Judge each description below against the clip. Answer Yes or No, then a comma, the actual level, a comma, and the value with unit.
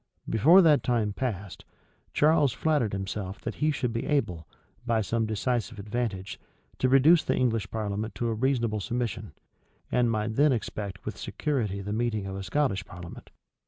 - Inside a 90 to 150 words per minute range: No, average, 160 wpm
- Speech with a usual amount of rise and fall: Yes, average, 4.2 semitones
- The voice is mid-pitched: No, low, 115 Hz